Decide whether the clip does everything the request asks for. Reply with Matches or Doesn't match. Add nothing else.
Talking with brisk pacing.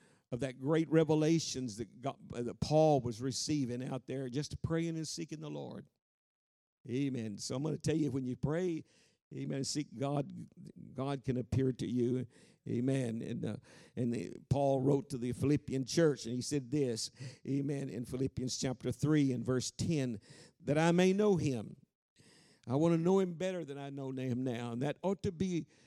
Doesn't match